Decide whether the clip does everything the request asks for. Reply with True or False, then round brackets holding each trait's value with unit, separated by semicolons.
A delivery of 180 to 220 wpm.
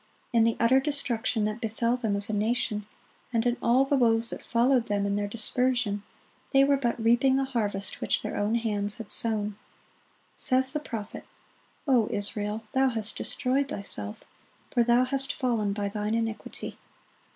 False (170 wpm)